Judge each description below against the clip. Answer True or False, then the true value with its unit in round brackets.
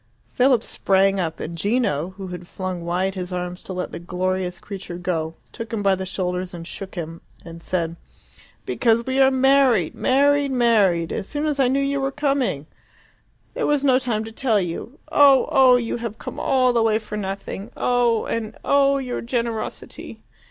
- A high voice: True (215 Hz)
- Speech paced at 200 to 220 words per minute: False (185 wpm)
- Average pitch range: False (6.1 semitones)